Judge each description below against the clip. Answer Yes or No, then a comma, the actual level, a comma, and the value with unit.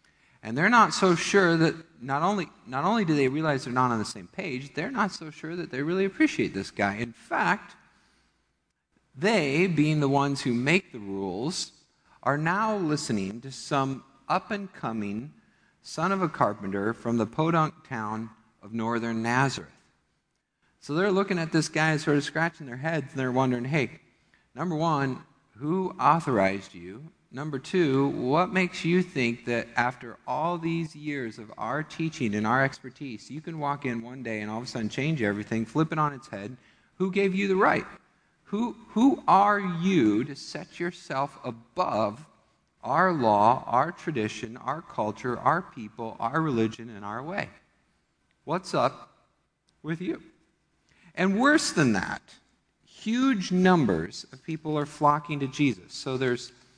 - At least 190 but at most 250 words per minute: No, average, 165 wpm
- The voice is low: No, medium, 145 Hz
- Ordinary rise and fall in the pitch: No, wide, 6.1 semitones